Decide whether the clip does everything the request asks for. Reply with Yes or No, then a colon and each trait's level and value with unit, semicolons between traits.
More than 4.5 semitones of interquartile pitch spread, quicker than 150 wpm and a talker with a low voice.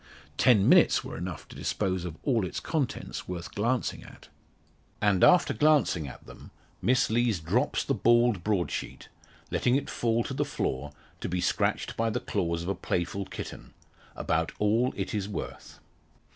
Yes: wide, 5.4 semitones; average, 165 wpm; low, 105 Hz